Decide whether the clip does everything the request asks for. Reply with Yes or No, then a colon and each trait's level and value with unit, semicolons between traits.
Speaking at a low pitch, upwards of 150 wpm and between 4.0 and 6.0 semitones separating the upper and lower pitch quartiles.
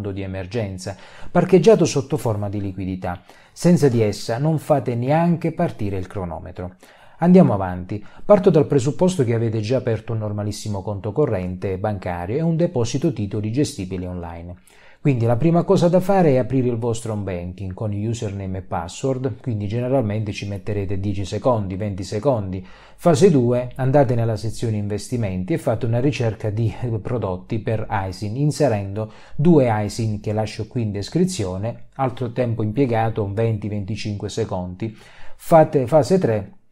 No: low, 115 Hz; average, 145 wpm; average, 5.2 semitones